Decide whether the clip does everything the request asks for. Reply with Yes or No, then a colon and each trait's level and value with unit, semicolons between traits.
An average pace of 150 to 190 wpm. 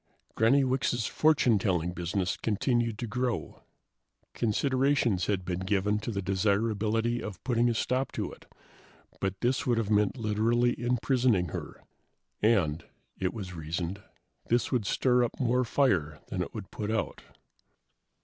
No: average, 140 wpm